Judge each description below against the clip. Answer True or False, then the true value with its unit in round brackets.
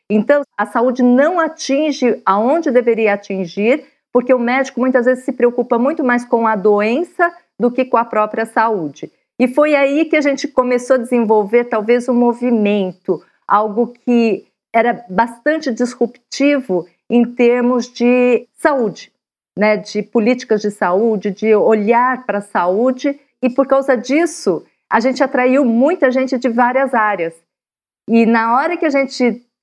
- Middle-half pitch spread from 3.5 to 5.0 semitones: False (3.0 semitones)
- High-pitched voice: True (245 Hz)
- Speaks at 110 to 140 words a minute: False (150 wpm)